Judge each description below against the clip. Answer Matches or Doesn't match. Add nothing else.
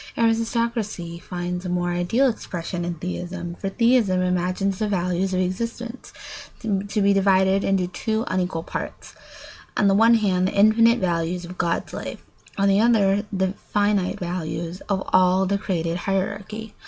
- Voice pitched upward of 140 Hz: Matches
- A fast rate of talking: Doesn't match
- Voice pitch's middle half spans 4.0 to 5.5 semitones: Doesn't match